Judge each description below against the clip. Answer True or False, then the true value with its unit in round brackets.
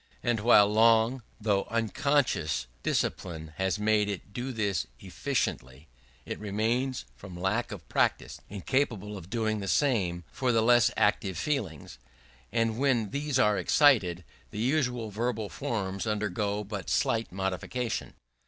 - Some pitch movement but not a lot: True (3.9 semitones)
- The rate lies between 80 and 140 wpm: True (135 wpm)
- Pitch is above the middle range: False (110 Hz)